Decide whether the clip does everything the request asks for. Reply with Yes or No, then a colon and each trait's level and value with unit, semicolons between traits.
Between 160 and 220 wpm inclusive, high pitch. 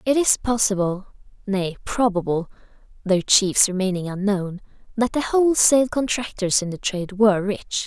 No: slow, 135 wpm; high, 205 Hz